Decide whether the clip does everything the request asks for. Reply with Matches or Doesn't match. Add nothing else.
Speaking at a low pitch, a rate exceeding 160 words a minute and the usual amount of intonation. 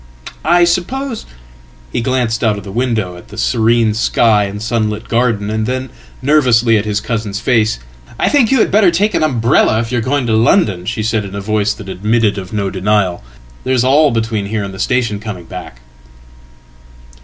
Matches